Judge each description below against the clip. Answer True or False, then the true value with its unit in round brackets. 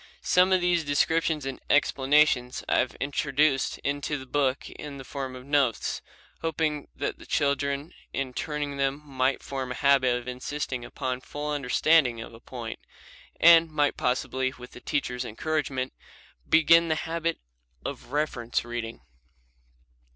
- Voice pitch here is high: False (140 Hz)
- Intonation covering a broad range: False (2.9 semitones)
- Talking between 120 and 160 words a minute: True (150 wpm)